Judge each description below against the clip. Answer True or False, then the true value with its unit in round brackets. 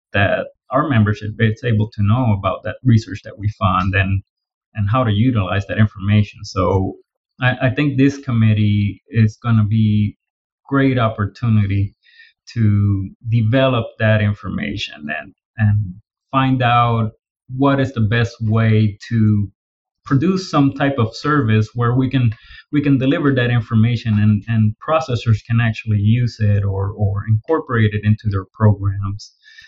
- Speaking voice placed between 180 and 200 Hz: False (110 Hz)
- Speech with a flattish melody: False (3.3 semitones)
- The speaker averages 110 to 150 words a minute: True (145 wpm)